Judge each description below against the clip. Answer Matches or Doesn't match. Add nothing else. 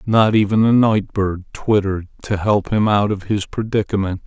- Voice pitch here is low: Matches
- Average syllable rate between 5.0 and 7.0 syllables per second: Doesn't match